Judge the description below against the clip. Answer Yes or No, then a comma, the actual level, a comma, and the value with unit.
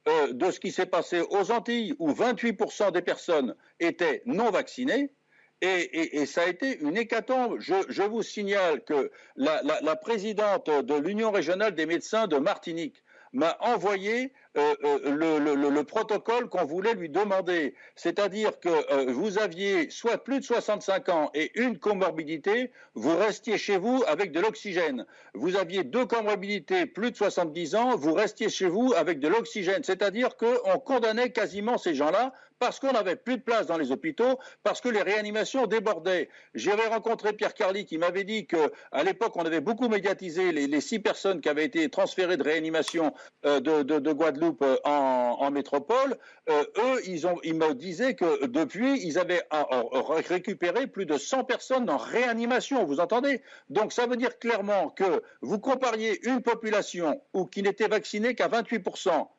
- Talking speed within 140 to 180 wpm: Yes, average, 175 wpm